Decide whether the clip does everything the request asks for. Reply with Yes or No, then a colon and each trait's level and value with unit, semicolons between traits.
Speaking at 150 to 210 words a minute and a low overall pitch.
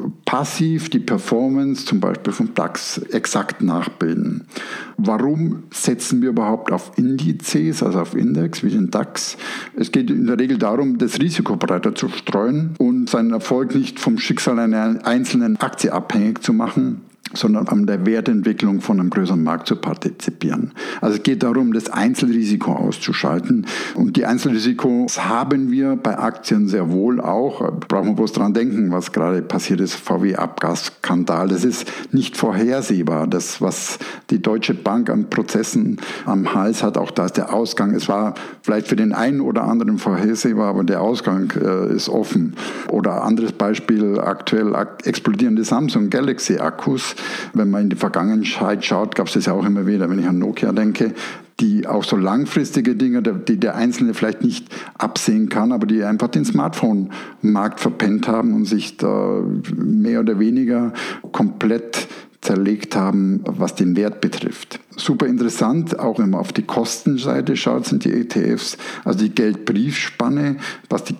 No: average, 160 wpm; high, 215 Hz